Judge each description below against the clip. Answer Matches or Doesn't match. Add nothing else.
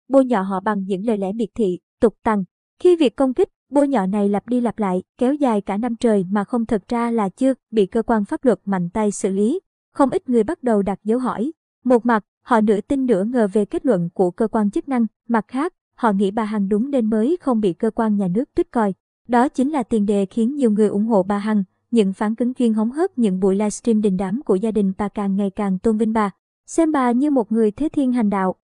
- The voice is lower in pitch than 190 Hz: Doesn't match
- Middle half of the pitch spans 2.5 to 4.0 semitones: Matches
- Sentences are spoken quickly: Matches